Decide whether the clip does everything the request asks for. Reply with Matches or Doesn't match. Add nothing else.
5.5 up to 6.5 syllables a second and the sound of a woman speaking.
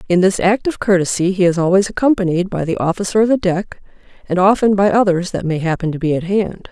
Matches